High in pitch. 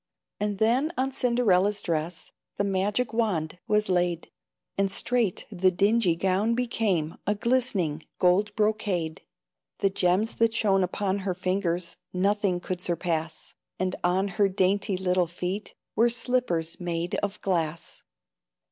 Yes: high, 195 Hz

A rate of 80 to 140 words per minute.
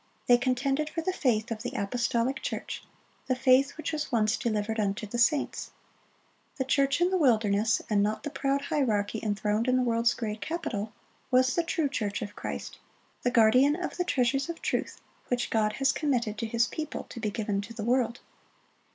No: average, 185 wpm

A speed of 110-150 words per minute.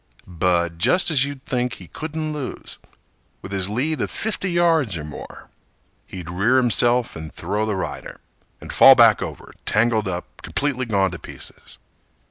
No: average, 160 wpm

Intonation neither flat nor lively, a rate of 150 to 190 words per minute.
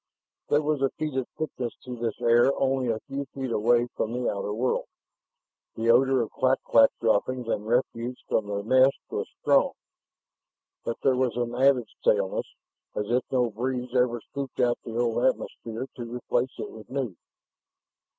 No: narrow, 2.2 semitones; average, 170 wpm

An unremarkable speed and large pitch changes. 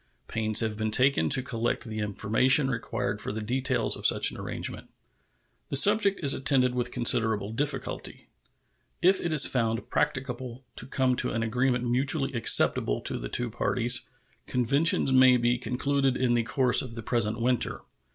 No: average, 165 wpm; average, 2.8 semitones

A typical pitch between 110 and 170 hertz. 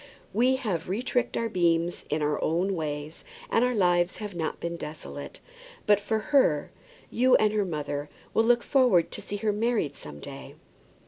No: high, 195 Hz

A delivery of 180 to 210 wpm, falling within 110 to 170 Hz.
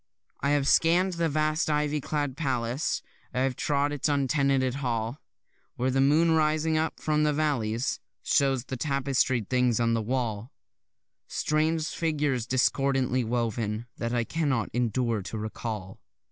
No: average, 145 wpm; low, 135 Hz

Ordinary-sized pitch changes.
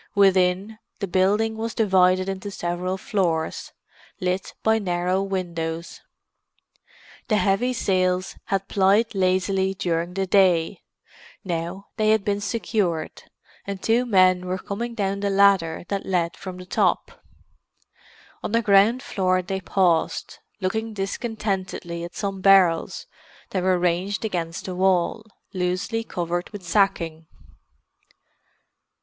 No: narrow, 2.0 semitones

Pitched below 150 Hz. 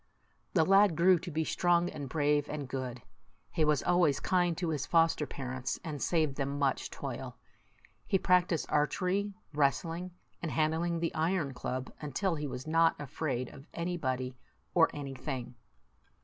No: medium, 155 Hz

